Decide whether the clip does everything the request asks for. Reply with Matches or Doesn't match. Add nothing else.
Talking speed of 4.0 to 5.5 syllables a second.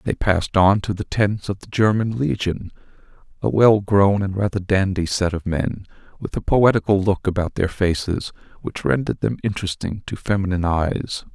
Matches